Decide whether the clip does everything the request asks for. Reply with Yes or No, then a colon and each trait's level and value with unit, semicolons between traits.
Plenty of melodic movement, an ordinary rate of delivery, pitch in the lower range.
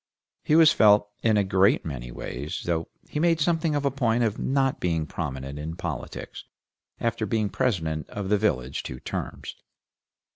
Yes: wide, 8.8 semitones; average, 170 wpm; low, 105 Hz